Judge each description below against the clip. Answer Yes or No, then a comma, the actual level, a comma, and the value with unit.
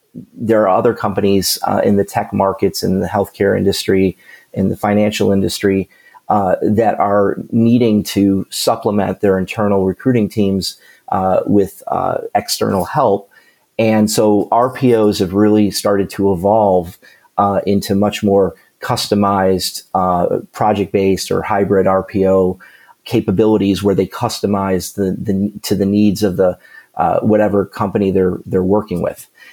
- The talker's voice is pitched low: Yes, low, 100 Hz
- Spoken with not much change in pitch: Yes, narrow, 1.6 semitones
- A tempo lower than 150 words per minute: Yes, average, 140 wpm